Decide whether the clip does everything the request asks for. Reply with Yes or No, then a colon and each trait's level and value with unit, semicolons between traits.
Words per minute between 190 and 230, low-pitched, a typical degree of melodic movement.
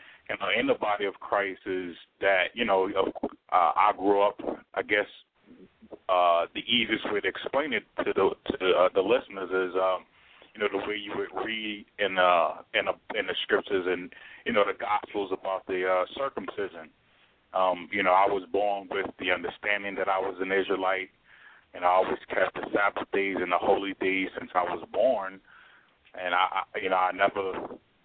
No: average, 195 wpm; very low, 95 Hz; narrow, 1.5 semitones